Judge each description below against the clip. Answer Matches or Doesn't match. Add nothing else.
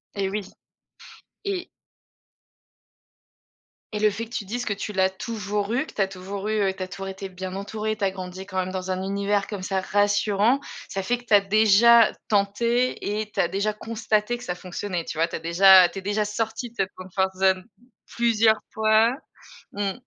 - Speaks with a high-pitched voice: Matches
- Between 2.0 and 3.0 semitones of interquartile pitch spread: Matches